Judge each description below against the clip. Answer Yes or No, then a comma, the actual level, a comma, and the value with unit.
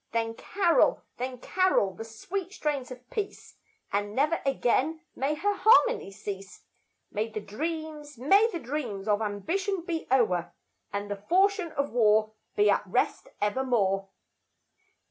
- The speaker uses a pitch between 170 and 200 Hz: No, very high, 255 Hz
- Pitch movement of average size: No, wide, 8.2 semitones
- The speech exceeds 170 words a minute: No, average, 140 wpm